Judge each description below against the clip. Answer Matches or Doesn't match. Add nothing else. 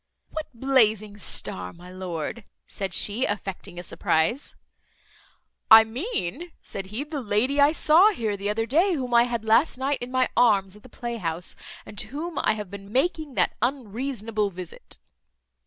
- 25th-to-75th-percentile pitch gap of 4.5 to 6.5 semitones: Matches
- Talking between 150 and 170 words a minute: Matches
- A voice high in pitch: Matches